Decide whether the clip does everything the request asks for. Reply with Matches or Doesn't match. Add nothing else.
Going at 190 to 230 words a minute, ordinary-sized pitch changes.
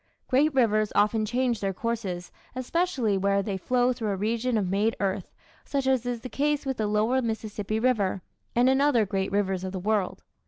Matches